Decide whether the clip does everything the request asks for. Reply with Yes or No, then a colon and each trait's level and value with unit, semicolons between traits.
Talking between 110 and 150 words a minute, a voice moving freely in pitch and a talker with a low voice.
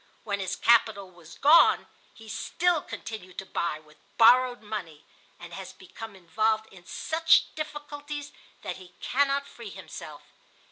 No: average, 140 wpm; wide, 7.4 semitones; high, 220 Hz